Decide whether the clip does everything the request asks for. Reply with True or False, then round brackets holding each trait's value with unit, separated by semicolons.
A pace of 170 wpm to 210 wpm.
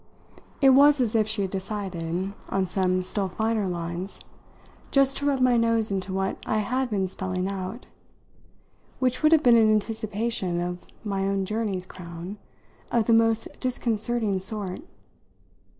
False (150 wpm)